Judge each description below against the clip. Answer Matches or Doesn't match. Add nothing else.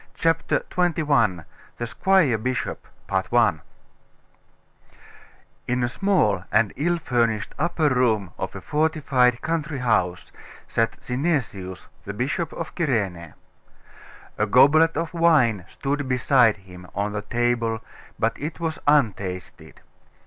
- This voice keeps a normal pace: Doesn't match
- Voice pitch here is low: Matches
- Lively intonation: Matches